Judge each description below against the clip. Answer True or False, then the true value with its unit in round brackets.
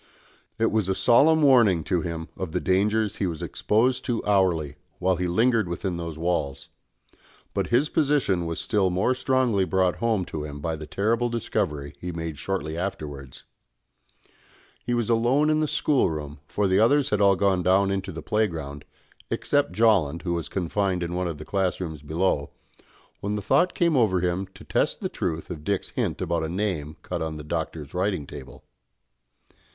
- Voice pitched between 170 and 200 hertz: False (95 Hz)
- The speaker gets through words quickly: False (180 wpm)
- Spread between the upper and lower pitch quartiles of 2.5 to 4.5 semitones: False (5.2 semitones)